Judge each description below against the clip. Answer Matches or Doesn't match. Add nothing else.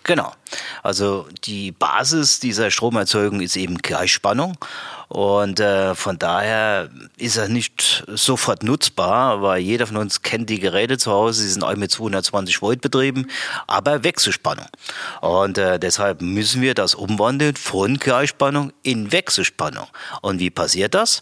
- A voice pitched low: Matches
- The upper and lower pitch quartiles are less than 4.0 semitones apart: Doesn't match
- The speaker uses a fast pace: Doesn't match